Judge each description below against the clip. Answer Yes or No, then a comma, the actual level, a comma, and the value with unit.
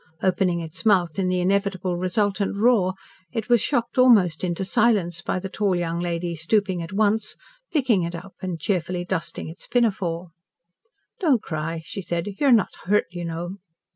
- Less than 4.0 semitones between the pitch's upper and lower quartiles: Yes, average, 3.2 semitones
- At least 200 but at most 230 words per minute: No, average, 170 wpm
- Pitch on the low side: No, medium, 185 Hz